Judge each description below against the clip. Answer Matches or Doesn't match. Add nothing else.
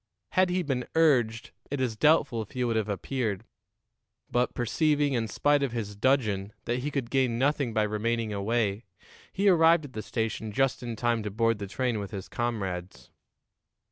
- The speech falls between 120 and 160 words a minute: Doesn't match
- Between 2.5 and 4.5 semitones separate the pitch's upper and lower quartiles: Matches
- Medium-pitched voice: Doesn't match